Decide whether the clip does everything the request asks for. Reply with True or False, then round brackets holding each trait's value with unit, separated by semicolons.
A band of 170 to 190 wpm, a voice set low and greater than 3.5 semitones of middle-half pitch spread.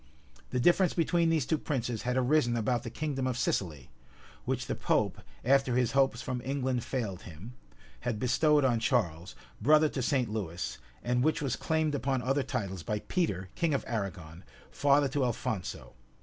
True (175 wpm; 125 Hz; 4.6 semitones)